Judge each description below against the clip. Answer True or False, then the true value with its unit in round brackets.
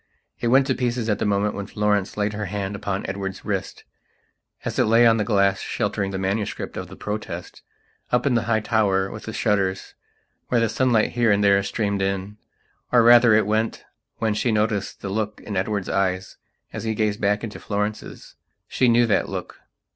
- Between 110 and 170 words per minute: False (195 wpm)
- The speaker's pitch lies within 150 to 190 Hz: False (105 Hz)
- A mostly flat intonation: True (2.2 semitones)